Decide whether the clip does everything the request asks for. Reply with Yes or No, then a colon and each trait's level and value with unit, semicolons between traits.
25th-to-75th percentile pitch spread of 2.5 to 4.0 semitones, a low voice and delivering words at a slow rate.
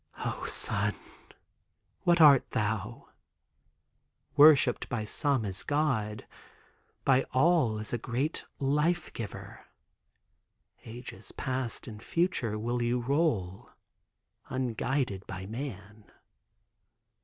No: average, 4.8 semitones; low, 125 Hz; slow, 95 wpm